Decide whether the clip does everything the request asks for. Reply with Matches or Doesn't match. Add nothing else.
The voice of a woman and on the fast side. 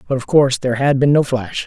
Doesn't match